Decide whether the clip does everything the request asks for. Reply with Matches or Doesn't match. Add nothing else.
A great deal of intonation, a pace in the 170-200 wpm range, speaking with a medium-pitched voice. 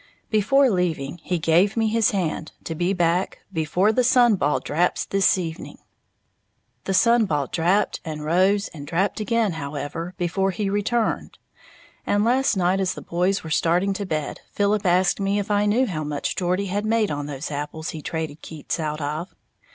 Doesn't match